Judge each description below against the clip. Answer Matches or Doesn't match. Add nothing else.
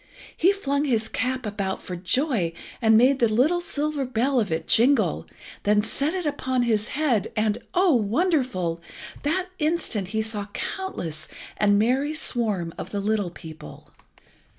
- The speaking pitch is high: Matches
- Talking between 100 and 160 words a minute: Matches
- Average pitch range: Doesn't match